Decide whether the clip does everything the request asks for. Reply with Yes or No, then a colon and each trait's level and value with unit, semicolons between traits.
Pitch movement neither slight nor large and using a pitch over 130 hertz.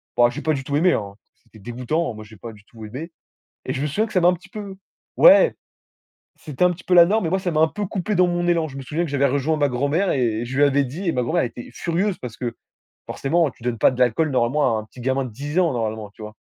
No: wide, 6.2 semitones; medium, 140 Hz